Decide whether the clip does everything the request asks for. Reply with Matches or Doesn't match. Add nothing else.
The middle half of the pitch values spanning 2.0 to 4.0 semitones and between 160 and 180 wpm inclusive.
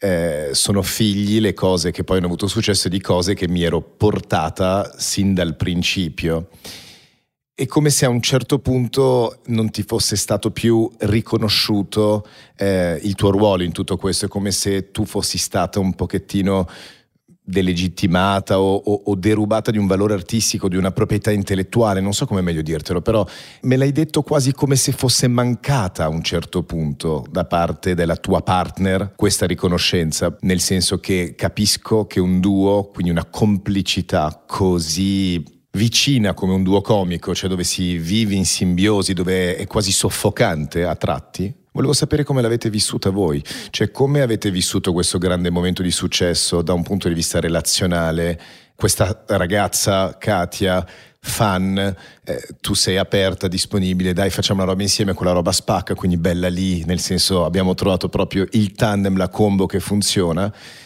Matches